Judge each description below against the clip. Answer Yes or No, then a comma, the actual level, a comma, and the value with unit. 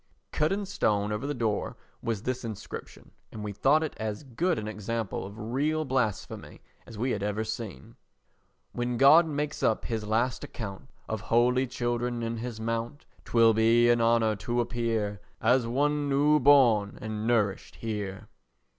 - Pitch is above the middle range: No, low, 115 Hz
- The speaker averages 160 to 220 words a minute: Yes, average, 165 wpm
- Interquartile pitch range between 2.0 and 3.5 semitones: Yes, average, 3.1 semitones